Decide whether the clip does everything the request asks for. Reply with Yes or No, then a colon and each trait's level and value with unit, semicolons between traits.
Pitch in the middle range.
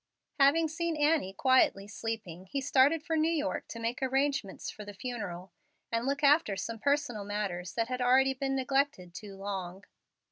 No: very high, 250 Hz